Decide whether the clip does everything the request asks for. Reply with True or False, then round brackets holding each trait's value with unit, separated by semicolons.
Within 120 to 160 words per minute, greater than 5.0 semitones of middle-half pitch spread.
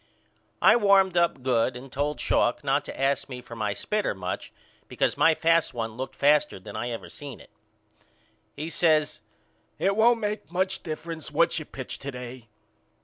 False (175 wpm; 5.4 semitones)